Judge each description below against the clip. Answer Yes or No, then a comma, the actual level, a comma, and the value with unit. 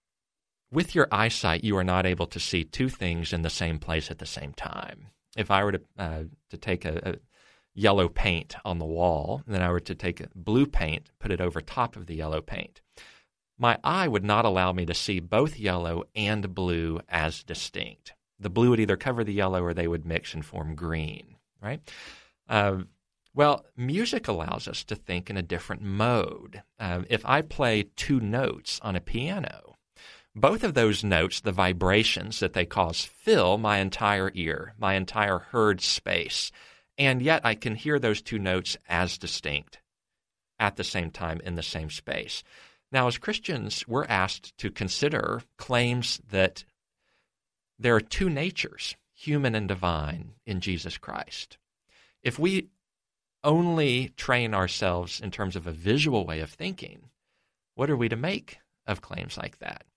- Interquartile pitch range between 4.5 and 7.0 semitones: Yes, average, 5.0 semitones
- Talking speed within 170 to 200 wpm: Yes, average, 175 wpm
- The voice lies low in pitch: Yes, low, 100 Hz